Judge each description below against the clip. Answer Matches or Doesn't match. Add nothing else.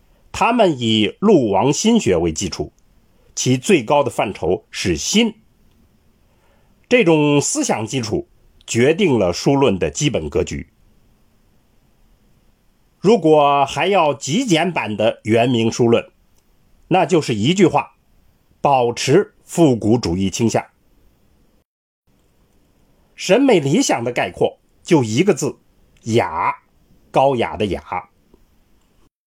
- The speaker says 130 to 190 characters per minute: Matches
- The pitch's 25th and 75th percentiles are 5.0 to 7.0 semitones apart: Doesn't match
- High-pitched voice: Doesn't match